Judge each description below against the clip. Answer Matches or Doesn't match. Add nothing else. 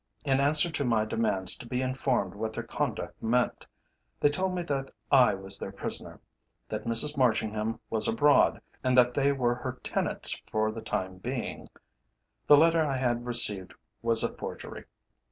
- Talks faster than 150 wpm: Matches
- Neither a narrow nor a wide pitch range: Matches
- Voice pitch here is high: Doesn't match